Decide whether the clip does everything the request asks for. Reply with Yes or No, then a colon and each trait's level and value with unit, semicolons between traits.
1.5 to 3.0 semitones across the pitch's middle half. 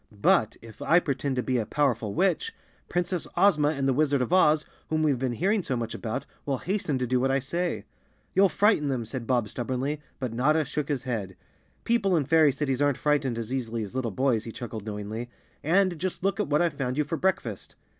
No: average, 4.7 semitones